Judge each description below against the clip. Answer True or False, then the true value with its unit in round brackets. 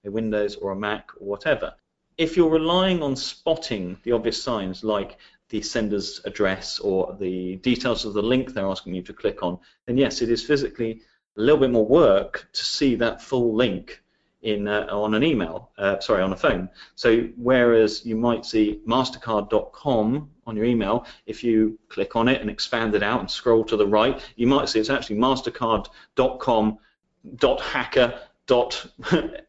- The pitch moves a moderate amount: True (3.2 semitones)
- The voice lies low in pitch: True (115 Hz)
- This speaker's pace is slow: False (175 wpm)